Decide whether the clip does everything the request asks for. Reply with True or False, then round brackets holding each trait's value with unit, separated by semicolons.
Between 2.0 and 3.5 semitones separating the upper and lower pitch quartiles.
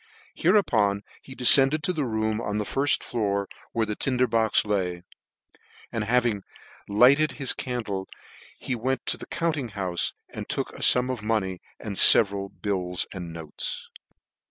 False (4.3 semitones)